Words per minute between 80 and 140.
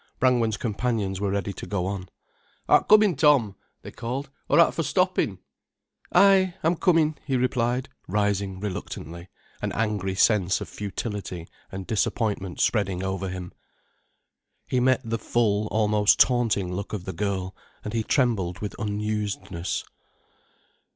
Yes: slow, 135 wpm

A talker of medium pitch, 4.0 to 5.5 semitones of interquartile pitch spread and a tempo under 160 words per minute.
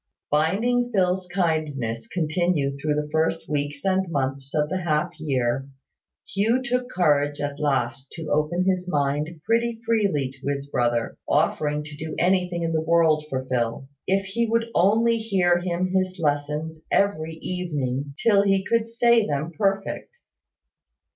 Yes: medium, 160 Hz; average, 5.0 semitones; average, 150 wpm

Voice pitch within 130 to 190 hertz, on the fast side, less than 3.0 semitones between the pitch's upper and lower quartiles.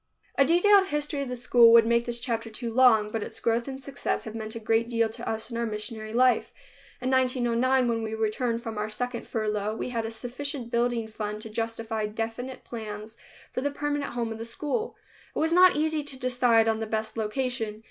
No: high, 235 Hz; fast, 215 wpm; narrow, 2.6 semitones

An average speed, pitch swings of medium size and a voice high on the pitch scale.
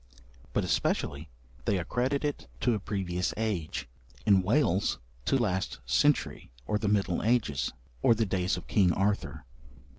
No: average, 145 wpm; average, 3.9 semitones; low, 100 Hz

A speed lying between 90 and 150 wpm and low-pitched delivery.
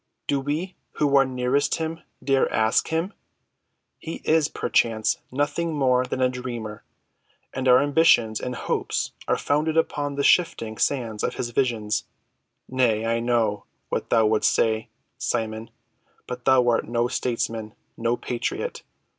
Yes: average, 140 wpm; low, 125 Hz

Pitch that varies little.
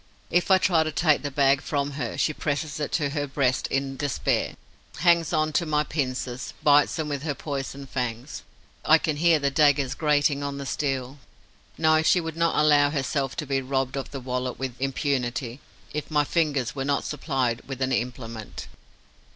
Yes: narrow, 2.3 semitones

